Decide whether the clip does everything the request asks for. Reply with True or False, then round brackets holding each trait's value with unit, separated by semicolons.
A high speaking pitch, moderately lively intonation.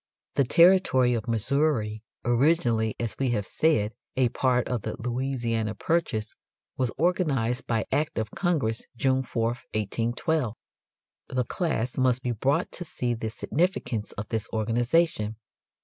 False (120 Hz; 4.0 semitones)